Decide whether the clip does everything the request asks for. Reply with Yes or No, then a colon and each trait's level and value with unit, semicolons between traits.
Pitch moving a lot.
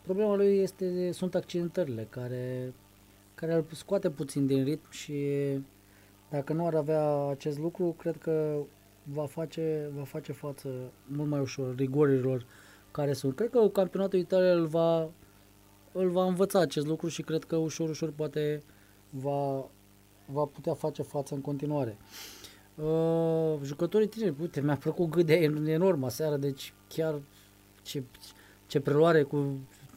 No: average, 4.0 semitones